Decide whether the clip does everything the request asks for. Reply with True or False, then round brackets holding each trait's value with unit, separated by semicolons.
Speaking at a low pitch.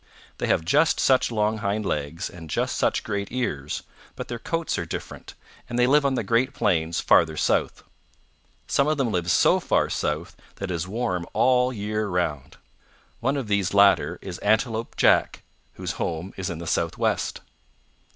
True (100 Hz)